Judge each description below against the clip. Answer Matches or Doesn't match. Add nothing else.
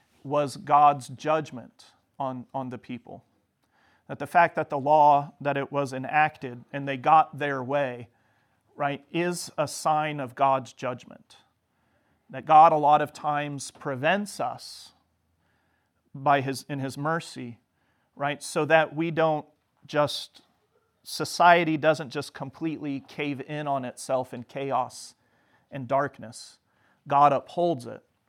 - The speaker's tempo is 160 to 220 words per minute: Doesn't match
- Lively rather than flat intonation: Doesn't match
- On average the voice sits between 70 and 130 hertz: Doesn't match